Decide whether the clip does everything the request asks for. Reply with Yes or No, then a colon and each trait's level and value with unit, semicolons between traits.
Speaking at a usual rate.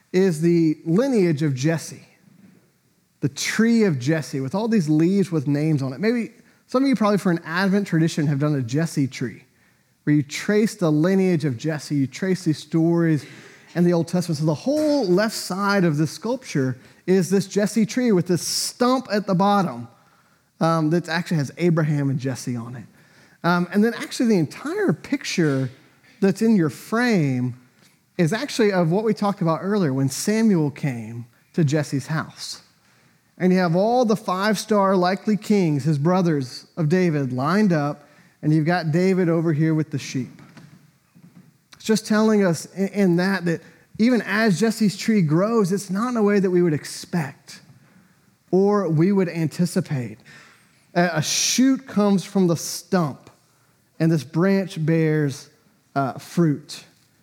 Yes: average, 165 wpm